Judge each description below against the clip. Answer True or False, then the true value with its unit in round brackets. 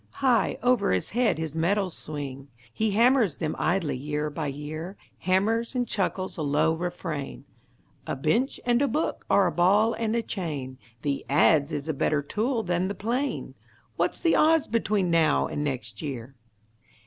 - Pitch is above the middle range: False (175 Hz)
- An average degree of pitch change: False (7.2 semitones)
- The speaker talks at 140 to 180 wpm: True (170 wpm)